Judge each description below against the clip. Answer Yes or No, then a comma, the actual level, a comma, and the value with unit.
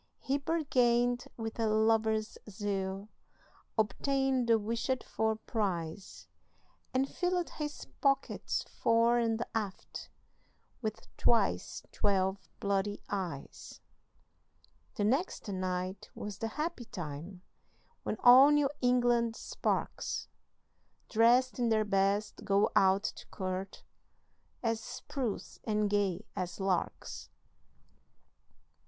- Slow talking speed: Yes, slow, 100 wpm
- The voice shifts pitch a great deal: No, average, 3.8 semitones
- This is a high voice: Yes, high, 220 Hz